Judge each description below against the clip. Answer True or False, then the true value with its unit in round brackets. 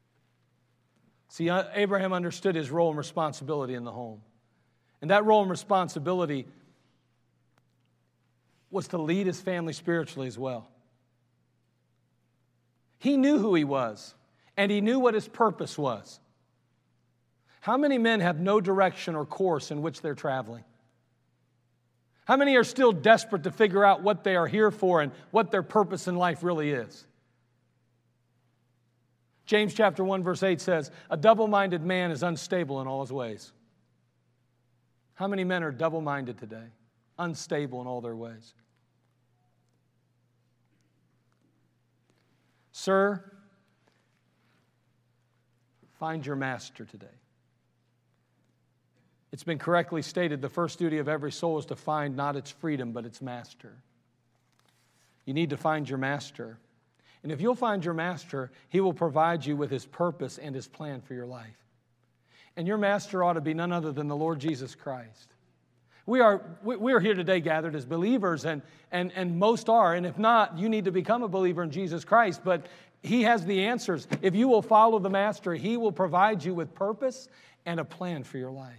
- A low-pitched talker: False (155 Hz)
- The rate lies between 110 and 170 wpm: True (155 wpm)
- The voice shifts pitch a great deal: True (7.4 semitones)